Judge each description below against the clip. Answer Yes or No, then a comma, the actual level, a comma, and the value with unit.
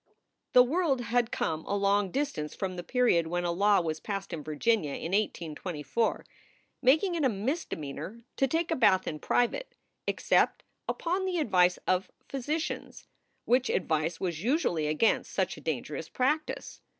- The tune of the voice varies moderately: No, wide, 7.8 semitones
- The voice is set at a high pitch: Yes, high, 205 Hz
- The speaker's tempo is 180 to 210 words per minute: No, average, 160 wpm